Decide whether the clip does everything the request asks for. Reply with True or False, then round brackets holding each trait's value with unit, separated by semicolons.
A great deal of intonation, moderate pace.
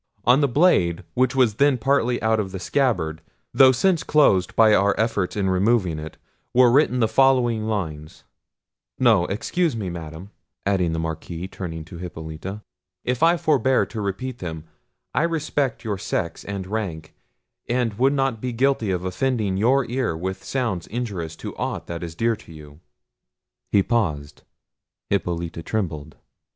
True (6.5 semitones; 155 wpm)